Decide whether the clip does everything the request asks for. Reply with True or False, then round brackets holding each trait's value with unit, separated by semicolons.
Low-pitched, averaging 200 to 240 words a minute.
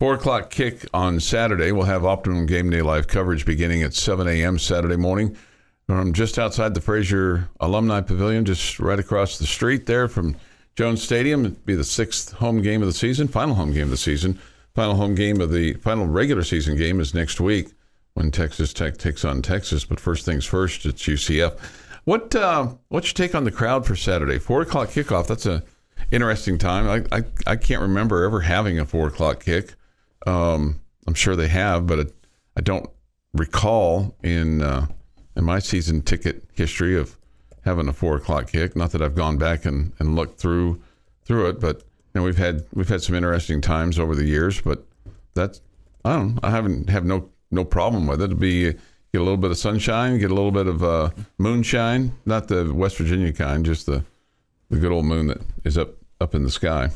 True (90 Hz; 205 wpm)